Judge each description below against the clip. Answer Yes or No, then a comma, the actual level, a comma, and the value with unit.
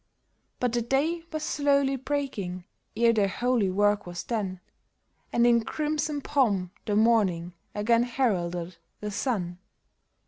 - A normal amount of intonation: No, wide, 6.0 semitones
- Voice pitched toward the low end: No, high, 230 Hz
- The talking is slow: Yes, slow, 130 wpm